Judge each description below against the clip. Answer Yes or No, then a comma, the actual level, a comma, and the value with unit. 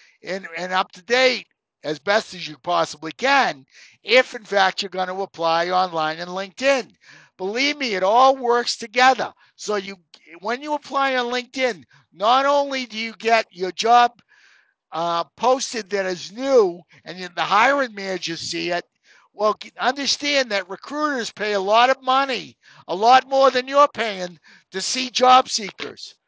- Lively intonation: Yes, wide, 6.0 semitones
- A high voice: Yes, high, 215 Hz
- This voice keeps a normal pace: Yes, average, 160 wpm